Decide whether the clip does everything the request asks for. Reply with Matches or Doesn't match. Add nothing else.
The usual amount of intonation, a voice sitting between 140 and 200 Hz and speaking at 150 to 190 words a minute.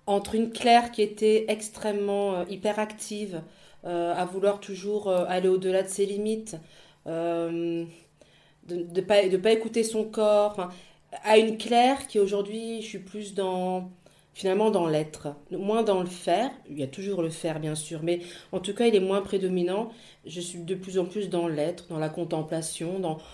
Matches